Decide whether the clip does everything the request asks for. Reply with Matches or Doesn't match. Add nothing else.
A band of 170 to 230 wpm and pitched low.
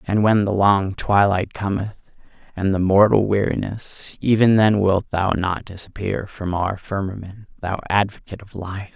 Doesn't match